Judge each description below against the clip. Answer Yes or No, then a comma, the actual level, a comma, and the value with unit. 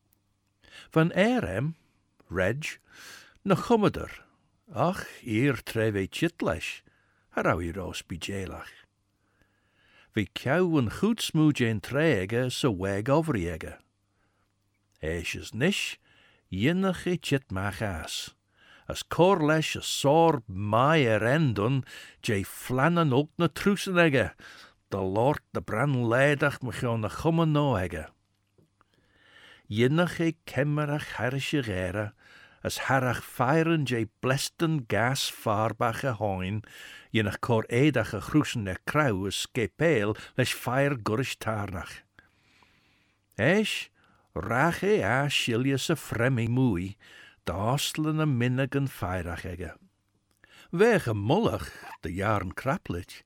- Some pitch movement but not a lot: No, wide, 6.7 semitones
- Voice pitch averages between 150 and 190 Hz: No, low, 120 Hz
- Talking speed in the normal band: No, slow, 90 wpm